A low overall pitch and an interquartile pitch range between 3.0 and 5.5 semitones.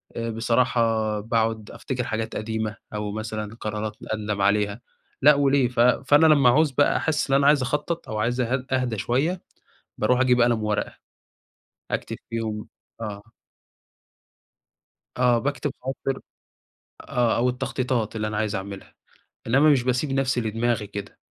Yes: low, 120 Hz; average, 3.3 semitones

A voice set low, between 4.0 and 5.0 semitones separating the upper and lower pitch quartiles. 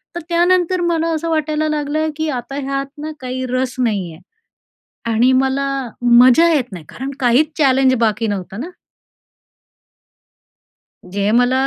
No: very high, 265 Hz; average, 4.3 semitones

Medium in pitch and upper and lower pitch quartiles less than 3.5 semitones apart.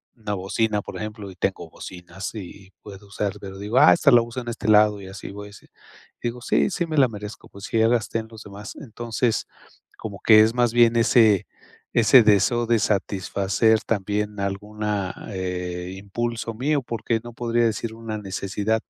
No: low, 110 Hz; average, 2.7 semitones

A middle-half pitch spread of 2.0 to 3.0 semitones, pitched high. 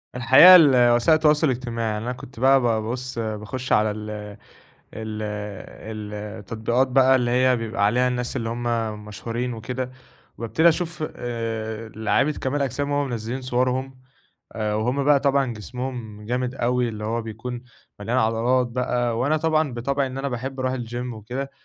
No: narrow, 2.5 semitones; low, 125 Hz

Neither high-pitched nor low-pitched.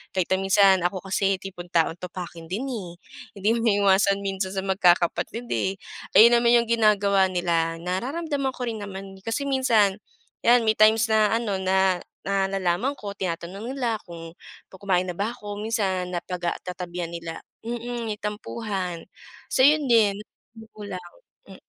No: high, 195 Hz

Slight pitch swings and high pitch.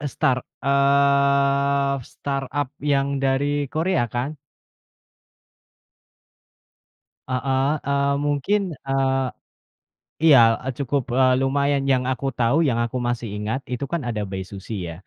No: narrow, 1.9 semitones; low, 135 Hz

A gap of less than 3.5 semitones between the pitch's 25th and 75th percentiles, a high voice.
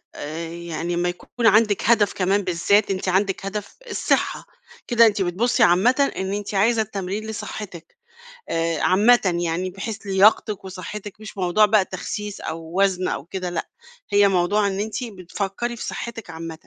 Yes: average, 3.1 semitones; high, 195 Hz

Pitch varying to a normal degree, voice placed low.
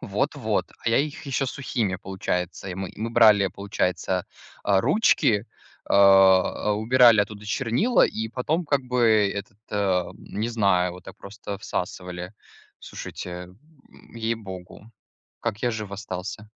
Yes: average, 3.4 semitones; low, 105 Hz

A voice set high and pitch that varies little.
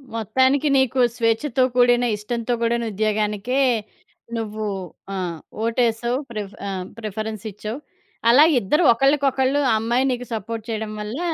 No: high, 230 Hz; average, 3.0 semitones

